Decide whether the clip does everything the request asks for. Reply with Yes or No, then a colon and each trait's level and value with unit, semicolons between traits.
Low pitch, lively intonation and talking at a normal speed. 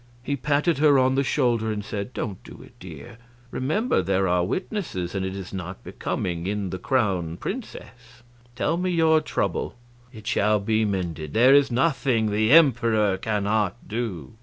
Yes: low, 110 Hz; wide, 5.8 semitones; average, 165 wpm